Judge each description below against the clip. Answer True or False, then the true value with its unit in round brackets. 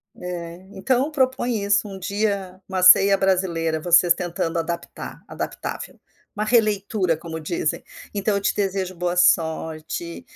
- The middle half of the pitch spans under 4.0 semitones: True (3.0 semitones)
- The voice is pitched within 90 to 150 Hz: False (185 Hz)